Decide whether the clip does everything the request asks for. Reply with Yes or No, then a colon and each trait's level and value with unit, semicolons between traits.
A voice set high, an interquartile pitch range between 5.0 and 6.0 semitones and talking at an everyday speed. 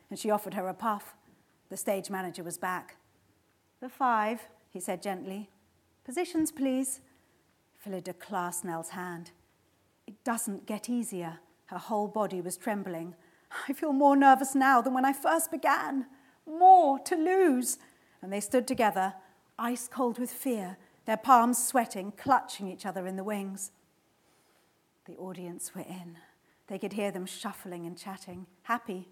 Yes: high, 205 Hz; wide, 5.5 semitones; average, 150 wpm